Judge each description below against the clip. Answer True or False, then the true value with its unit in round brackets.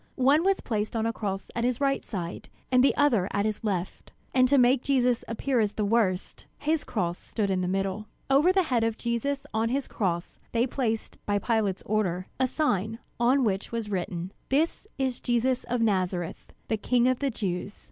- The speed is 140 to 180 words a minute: False (200 wpm)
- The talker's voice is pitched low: False (230 Hz)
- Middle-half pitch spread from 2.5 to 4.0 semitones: False (4.4 semitones)